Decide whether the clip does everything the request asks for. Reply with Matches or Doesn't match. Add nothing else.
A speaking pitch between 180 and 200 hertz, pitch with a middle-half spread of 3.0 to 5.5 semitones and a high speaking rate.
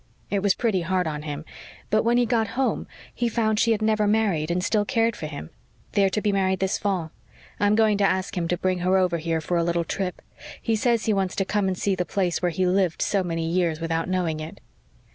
Matches